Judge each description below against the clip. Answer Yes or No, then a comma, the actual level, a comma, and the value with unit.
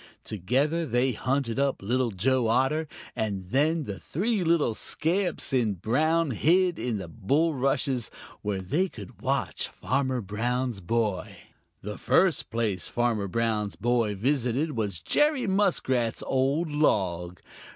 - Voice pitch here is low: Yes, low, 125 Hz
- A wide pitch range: Yes, wide, 6.2 semitones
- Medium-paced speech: No, slow, 130 wpm